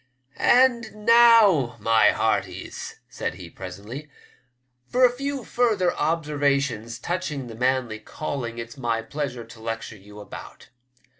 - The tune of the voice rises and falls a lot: Yes, wide, 8.6 semitones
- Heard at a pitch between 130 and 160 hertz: Yes, low, 135 Hz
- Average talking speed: No, slow, 125 wpm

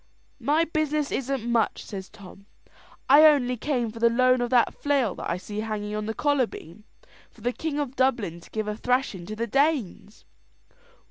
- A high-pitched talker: Yes, high, 240 Hz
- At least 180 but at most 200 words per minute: Yes, average, 190 wpm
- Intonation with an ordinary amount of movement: Yes, average, 4.5 semitones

